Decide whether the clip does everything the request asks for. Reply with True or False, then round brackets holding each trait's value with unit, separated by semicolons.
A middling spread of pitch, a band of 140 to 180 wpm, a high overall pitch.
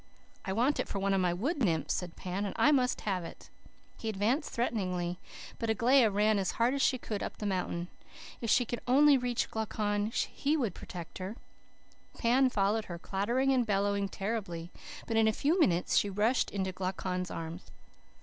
False (4.4 semitones; 190 wpm; 210 Hz)